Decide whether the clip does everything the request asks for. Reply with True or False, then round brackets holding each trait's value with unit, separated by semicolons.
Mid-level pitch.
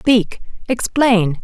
False (220 Hz)